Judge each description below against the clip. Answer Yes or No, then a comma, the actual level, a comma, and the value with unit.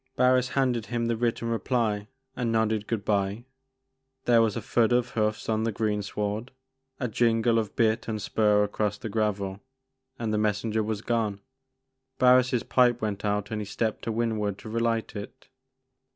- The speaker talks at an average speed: Yes, average, 165 wpm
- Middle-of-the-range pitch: No, low, 110 Hz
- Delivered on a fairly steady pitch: Yes, narrow, 2.0 semitones